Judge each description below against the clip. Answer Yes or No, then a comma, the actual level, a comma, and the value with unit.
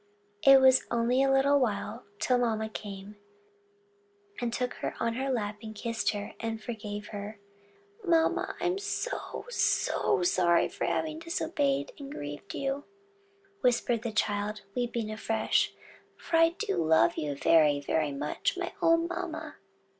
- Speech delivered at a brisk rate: No, slow, 135 wpm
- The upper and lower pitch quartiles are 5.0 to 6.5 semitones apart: Yes, average, 5.3 semitones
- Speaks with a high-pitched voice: Yes, high, 235 Hz